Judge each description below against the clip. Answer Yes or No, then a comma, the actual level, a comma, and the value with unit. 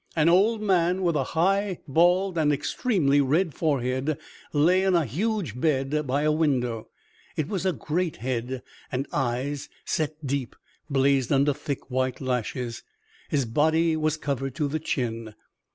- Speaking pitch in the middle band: Yes, medium, 145 Hz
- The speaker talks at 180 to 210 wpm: No, average, 150 wpm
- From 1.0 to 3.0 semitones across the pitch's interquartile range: No, average, 4.2 semitones